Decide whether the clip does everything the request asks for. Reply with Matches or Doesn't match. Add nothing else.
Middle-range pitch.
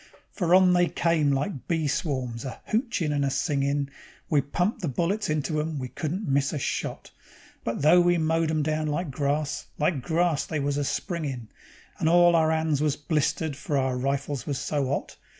Matches